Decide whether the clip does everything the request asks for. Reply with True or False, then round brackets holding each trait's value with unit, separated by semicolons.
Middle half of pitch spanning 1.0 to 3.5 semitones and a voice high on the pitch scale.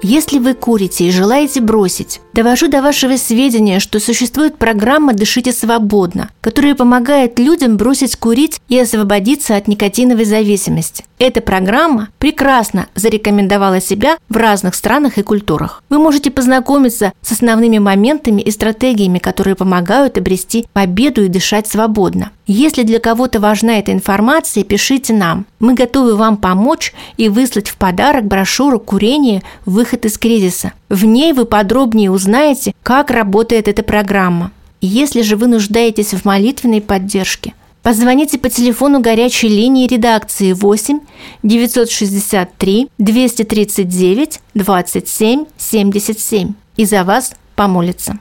False (3.9 semitones; 225 Hz)